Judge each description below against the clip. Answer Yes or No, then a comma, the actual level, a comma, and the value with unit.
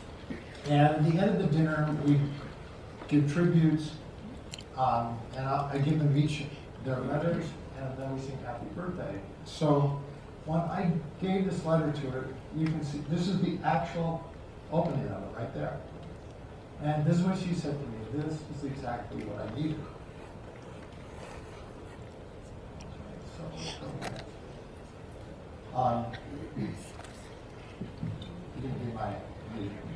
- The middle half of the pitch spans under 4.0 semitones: No, average, 4.7 semitones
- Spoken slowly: Yes, slow, 125 wpm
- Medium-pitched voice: Yes, medium, 145 Hz